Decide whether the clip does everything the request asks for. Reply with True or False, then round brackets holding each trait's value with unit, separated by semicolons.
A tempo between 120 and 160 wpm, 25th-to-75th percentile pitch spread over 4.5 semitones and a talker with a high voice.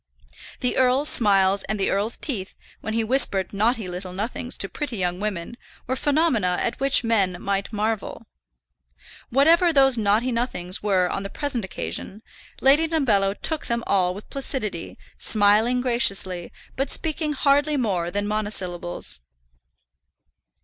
True (140 wpm; 5.1 semitones; 215 Hz)